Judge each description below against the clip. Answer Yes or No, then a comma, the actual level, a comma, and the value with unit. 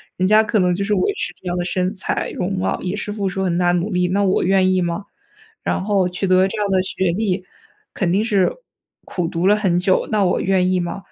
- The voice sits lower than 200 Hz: Yes, medium, 185 Hz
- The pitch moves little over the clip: Yes, narrow, 1.7 semitones